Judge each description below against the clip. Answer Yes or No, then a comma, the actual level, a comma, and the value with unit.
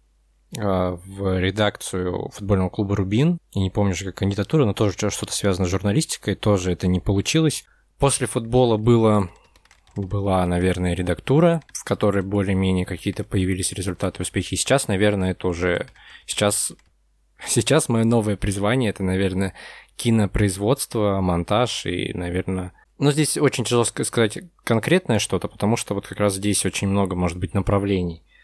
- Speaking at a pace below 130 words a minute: No, average, 140 wpm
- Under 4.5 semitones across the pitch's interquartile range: Yes, average, 3.5 semitones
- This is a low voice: Yes, low, 100 Hz